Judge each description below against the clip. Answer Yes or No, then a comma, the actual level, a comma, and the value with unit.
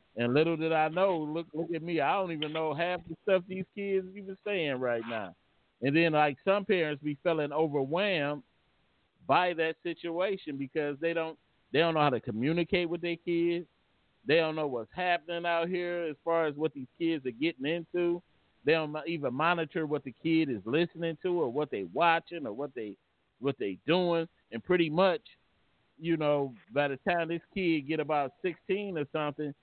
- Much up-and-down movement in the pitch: No, average, 2.7 semitones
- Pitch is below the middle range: No, medium, 165 Hz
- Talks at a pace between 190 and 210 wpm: Yes, average, 195 wpm